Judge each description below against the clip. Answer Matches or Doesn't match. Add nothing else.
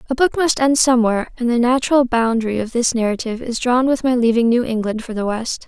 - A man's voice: Doesn't match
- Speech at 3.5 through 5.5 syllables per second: Doesn't match